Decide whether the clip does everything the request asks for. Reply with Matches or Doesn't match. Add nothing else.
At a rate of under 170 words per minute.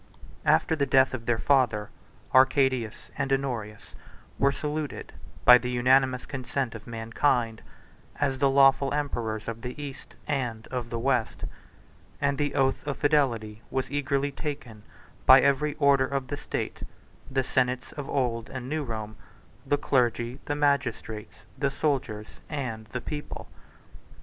Matches